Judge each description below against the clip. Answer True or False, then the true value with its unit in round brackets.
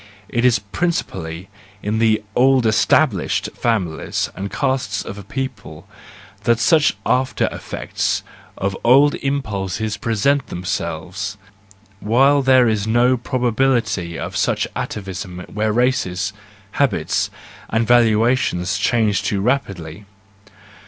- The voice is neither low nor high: False (110 Hz)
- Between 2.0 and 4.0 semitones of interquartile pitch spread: False (4.7 semitones)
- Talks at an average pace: False (110 wpm)